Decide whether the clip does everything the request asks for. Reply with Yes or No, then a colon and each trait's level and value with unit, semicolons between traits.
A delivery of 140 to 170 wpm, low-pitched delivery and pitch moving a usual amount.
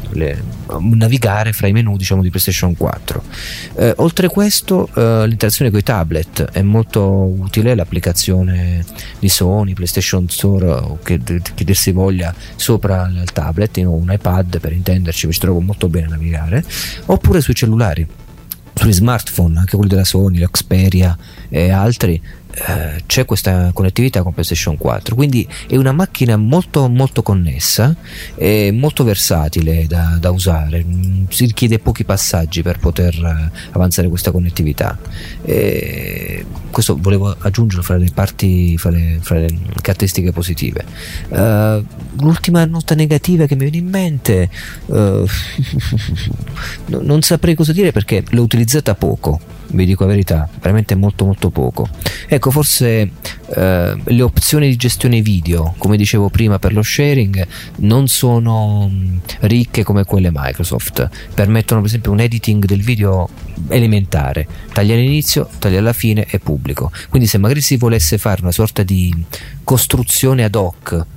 Yes: average, 145 wpm; low, 100 Hz; average, 4.6 semitones